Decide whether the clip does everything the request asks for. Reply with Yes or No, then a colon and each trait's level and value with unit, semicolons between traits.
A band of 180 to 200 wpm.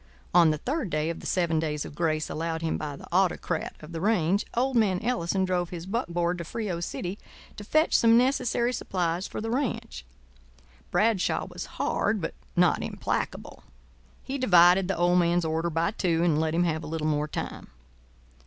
Yes: average, 185 wpm